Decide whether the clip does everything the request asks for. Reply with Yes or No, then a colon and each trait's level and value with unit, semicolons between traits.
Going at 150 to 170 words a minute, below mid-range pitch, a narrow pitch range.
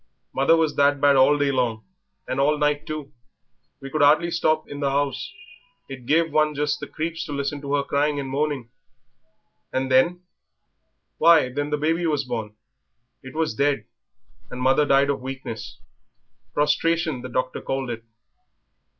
No: average, 165 wpm; medium, 145 Hz; narrow, 2.3 semitones